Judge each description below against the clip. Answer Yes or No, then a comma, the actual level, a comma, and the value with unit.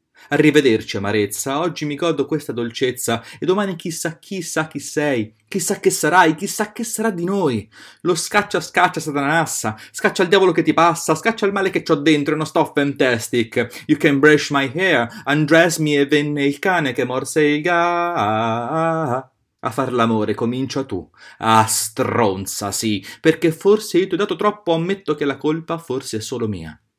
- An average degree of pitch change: No, wide, 6.0 semitones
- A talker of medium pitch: Yes, medium, 150 Hz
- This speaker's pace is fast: Yes, fast, 180 wpm